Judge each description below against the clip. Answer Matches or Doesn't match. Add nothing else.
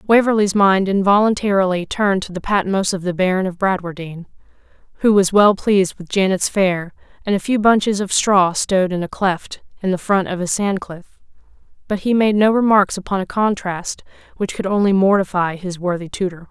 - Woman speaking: Matches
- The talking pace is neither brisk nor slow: Matches